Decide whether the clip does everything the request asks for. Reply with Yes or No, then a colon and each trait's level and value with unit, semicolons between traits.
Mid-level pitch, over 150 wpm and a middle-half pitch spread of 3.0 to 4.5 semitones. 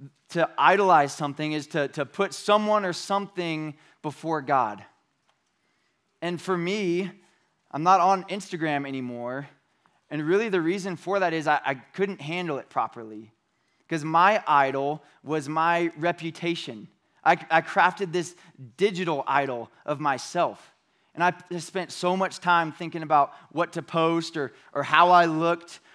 No: medium, 165 Hz; average, 145 wpm; average, 3.4 semitones